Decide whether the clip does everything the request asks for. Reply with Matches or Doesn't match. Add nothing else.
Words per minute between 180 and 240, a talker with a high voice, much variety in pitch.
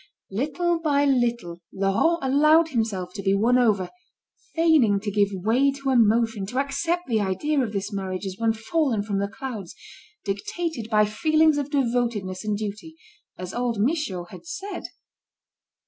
Doesn't match